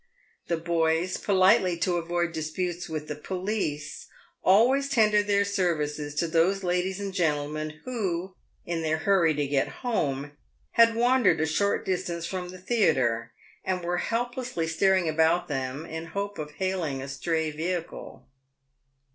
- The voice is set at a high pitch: No, medium, 175 Hz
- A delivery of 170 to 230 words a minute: No, average, 145 wpm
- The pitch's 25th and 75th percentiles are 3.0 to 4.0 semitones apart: Yes, average, 3.7 semitones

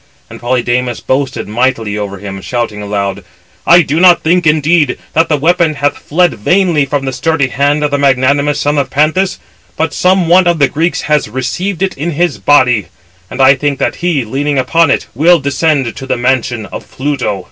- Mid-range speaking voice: Yes, medium, 145 Hz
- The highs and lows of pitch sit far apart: No, average, 4.2 semitones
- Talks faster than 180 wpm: Yes, average, 190 wpm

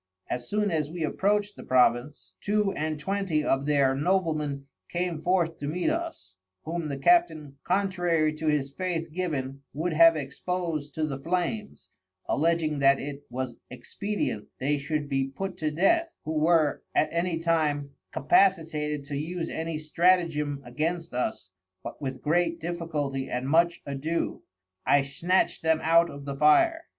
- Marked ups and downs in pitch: No, average, 3.7 semitones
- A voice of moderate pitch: Yes, medium, 155 Hz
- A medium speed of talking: Yes, average, 155 wpm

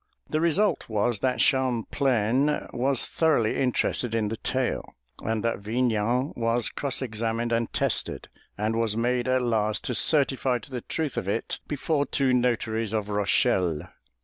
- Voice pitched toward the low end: Yes, low, 120 Hz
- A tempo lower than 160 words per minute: Yes, average, 150 wpm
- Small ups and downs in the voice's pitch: No, average, 3.0 semitones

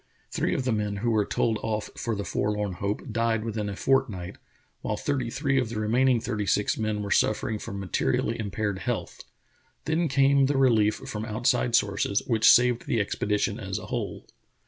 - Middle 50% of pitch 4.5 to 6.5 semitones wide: No, average, 2.9 semitones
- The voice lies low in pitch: Yes, low, 110 Hz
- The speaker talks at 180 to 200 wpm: Yes, average, 185 wpm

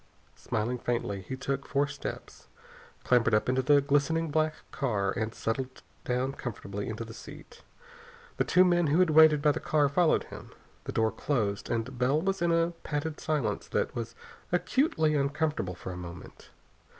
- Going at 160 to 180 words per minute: Yes, average, 170 wpm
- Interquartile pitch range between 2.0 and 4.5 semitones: No, average, 5.3 semitones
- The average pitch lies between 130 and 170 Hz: Yes, medium, 140 Hz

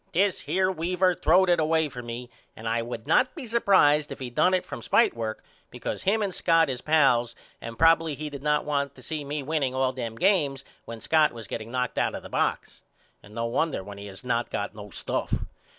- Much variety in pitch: Yes, wide, 5.8 semitones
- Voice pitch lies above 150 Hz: No, medium, 140 Hz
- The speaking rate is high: Yes, fast, 220 wpm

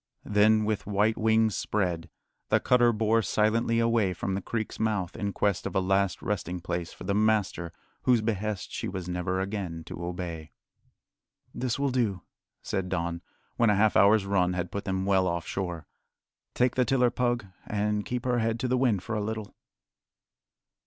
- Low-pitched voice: Yes, low, 105 Hz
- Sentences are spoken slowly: No, average, 180 wpm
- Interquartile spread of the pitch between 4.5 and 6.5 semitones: No, average, 3.3 semitones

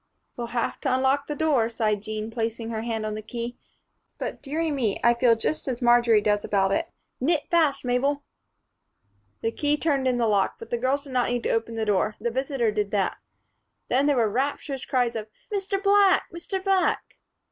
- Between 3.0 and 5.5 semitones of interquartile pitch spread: Yes, average, 4.1 semitones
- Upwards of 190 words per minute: Yes, average, 200 wpm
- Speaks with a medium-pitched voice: No, high, 240 Hz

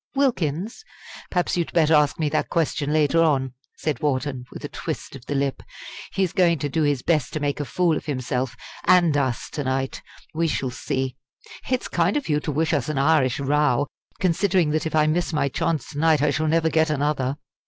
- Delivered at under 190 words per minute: No, fast, 205 wpm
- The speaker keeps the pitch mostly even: No, average, 3.0 semitones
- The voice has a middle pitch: Yes, medium, 150 Hz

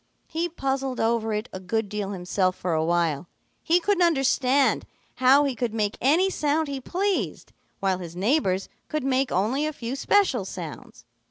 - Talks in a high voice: Yes, very high, 250 Hz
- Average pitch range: No, wide, 7.1 semitones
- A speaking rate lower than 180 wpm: Yes, average, 170 wpm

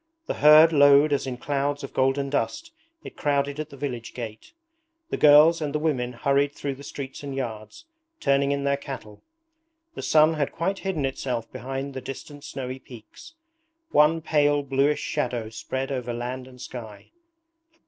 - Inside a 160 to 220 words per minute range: Yes, average, 170 wpm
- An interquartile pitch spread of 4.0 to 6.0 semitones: No, narrow, 2.4 semitones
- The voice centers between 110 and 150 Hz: Yes, medium, 140 Hz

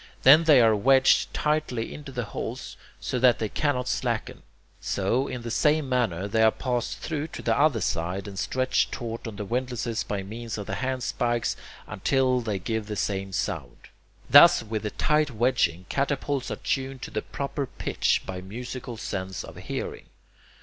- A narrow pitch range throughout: No, average, 4.0 semitones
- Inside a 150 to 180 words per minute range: Yes, average, 170 wpm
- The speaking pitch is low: Yes, low, 120 Hz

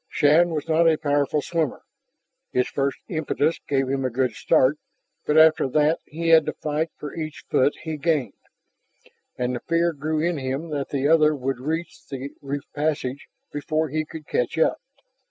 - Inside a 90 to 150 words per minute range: No, average, 175 wpm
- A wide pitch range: No, narrow, 2.6 semitones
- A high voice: No, medium, 150 Hz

